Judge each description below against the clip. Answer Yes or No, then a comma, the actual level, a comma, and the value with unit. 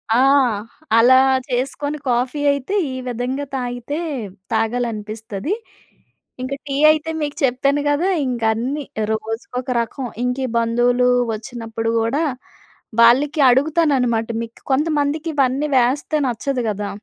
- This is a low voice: No, very high, 250 Hz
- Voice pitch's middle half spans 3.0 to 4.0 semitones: Yes, average, 3.5 semitones